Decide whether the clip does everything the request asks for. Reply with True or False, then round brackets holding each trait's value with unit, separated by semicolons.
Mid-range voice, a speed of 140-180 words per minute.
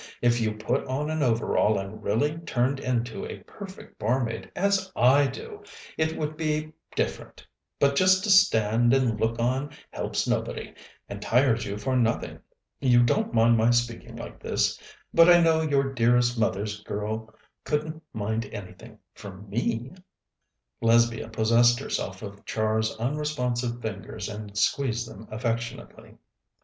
False (120 Hz; 145 wpm)